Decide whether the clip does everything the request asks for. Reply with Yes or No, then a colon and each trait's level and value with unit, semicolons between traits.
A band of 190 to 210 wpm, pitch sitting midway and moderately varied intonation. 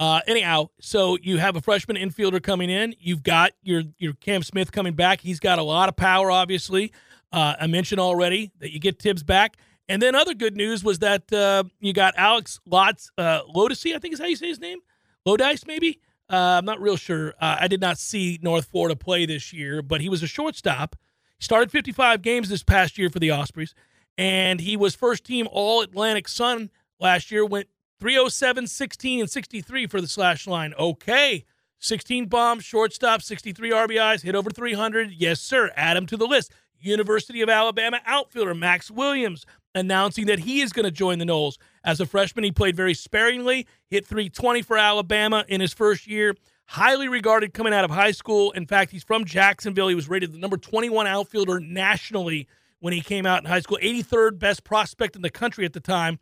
No: average, 200 wpm; high, 200 Hz; average, 3.8 semitones